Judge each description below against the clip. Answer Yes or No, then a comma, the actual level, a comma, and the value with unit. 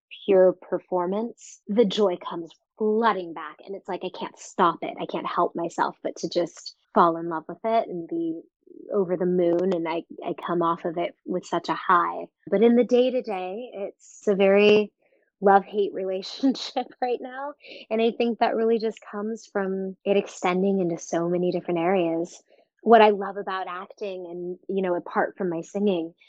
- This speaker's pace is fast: No, average, 190 wpm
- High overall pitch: Yes, high, 195 Hz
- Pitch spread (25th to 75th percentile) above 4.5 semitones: No, average, 3.9 semitones